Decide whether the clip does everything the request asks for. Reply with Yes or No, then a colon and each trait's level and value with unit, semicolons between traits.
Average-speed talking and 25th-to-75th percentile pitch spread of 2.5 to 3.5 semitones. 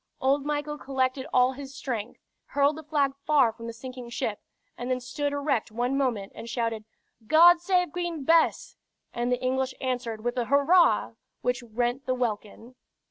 Yes: average, 170 wpm; average, 3.1 semitones